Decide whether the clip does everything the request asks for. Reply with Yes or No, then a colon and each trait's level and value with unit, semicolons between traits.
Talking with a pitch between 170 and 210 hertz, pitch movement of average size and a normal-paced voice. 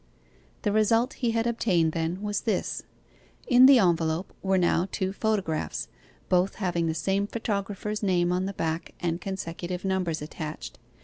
Yes: high, 190 Hz; average, 3.7 semitones; average, 150 wpm